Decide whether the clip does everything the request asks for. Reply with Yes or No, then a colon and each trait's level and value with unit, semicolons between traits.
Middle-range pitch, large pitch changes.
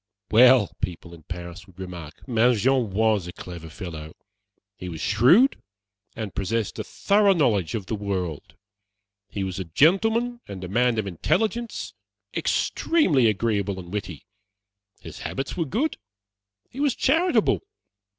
No: low, 105 Hz; wide, 7.3 semitones